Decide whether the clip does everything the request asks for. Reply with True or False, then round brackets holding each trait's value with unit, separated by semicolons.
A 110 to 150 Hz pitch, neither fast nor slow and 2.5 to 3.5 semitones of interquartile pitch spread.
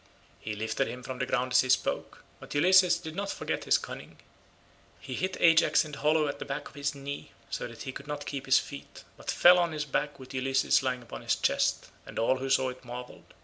False (140 Hz; 230 wpm; 2.8 semitones)